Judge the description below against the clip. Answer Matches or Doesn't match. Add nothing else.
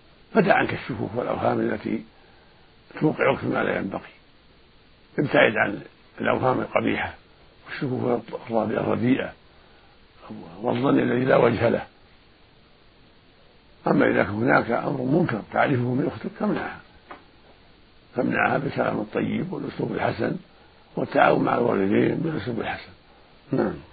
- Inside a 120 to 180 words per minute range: Doesn't match